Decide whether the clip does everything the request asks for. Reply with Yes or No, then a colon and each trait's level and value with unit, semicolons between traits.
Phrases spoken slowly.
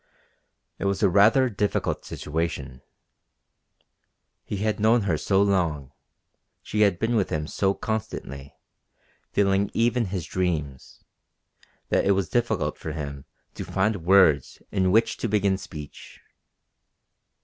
Yes: slow, 125 wpm